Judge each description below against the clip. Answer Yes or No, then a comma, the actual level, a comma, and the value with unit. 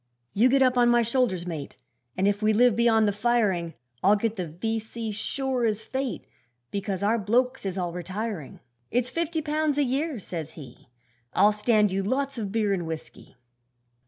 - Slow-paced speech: No, average, 180 wpm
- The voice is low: No, high, 220 Hz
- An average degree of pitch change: Yes, average, 4.3 semitones